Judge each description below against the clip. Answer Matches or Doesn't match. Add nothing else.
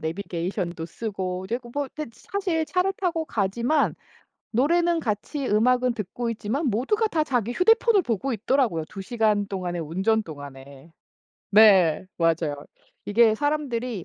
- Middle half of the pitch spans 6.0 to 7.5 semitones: Matches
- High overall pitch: Matches